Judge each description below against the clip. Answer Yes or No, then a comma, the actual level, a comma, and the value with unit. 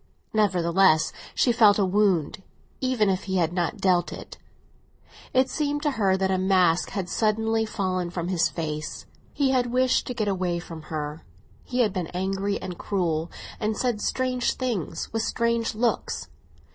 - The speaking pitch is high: Yes, high, 195 Hz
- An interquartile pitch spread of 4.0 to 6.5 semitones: Yes, average, 4.6 semitones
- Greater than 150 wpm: Yes, average, 165 wpm